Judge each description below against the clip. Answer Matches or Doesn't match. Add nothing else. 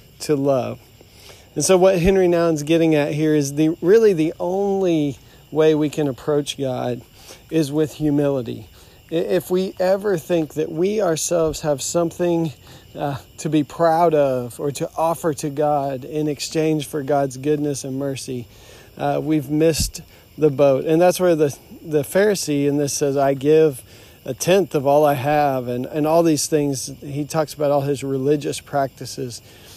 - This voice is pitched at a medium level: Matches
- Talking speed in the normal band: Matches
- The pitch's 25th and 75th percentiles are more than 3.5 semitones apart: Doesn't match